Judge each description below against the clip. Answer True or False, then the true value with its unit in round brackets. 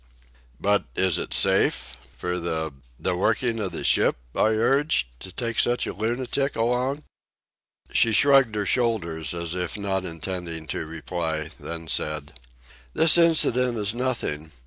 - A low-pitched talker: True (95 Hz)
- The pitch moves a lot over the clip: True (6.7 semitones)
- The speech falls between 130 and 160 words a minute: True (145 wpm)